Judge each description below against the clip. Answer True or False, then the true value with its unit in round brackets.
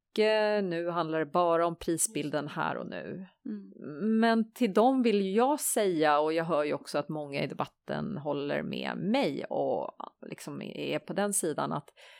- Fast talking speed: False (165 wpm)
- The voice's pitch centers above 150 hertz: True (190 Hz)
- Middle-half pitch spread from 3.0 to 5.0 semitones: False (5.6 semitones)